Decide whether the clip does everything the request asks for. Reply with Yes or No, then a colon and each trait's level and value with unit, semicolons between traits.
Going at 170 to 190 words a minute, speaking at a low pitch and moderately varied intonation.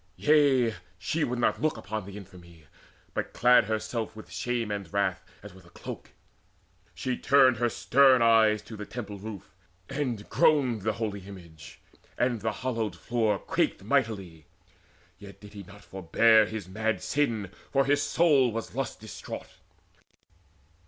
No: average, 150 wpm; low, 110 Hz; average, 3.6 semitones